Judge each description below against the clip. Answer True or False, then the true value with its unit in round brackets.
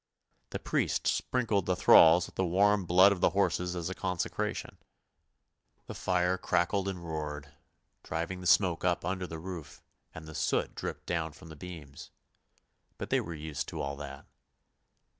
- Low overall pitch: True (90 Hz)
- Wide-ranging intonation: False (2.8 semitones)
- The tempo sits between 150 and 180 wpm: True (165 wpm)